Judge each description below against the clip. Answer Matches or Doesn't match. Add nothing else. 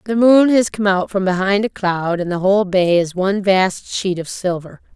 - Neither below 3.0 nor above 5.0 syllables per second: Matches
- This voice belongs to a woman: Matches